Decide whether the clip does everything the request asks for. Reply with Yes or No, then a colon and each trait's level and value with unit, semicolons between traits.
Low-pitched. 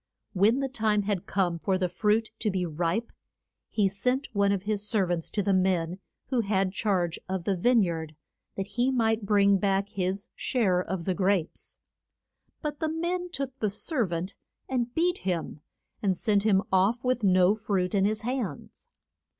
No: high, 200 Hz